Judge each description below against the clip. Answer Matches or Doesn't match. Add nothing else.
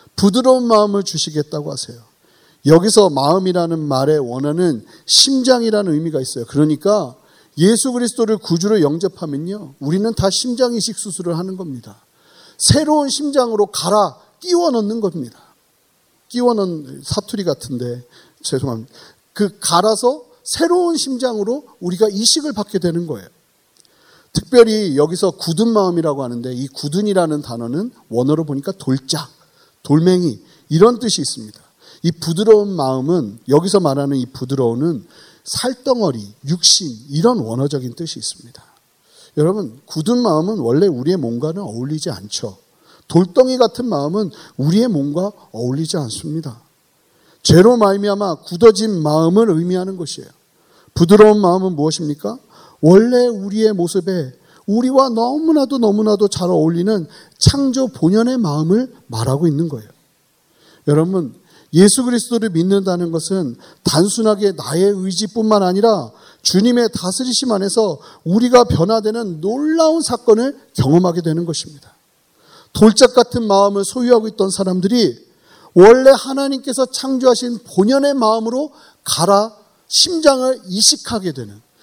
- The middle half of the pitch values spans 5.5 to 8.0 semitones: Matches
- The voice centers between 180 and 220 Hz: Matches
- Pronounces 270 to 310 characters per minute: Doesn't match